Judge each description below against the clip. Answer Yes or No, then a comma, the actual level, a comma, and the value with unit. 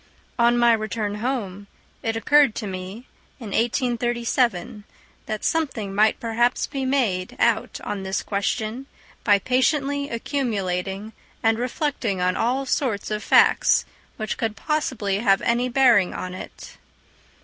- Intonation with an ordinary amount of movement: Yes, average, 3.9 semitones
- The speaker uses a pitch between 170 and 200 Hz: No, high, 225 Hz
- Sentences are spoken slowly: Yes, slow, 130 wpm